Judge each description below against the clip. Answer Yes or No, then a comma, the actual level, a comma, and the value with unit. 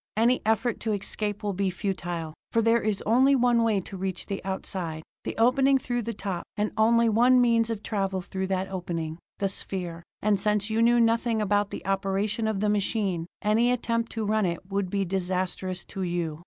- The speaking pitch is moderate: No, high, 205 Hz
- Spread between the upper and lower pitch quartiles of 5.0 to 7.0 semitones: No, average, 3.2 semitones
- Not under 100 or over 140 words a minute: No, average, 195 wpm